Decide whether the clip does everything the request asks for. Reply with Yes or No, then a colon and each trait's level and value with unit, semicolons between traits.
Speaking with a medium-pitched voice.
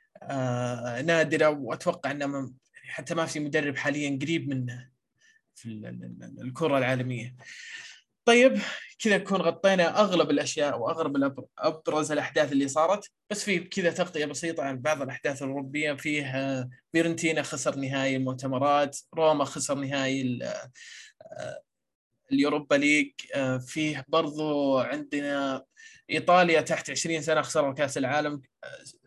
Yes: medium, 150 Hz